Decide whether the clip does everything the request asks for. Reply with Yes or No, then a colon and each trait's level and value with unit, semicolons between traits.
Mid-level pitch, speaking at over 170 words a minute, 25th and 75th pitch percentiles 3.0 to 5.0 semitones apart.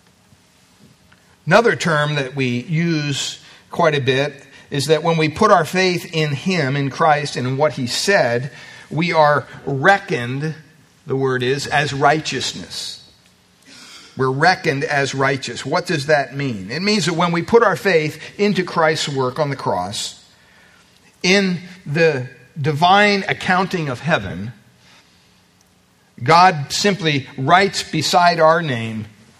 No: medium, 150 Hz; slow, 135 wpm; average, 4.2 semitones